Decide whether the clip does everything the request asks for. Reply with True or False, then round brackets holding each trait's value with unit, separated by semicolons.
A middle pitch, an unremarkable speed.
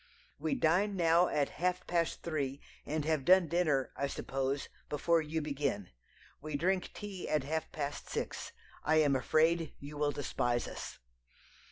True (155 Hz; 155 wpm)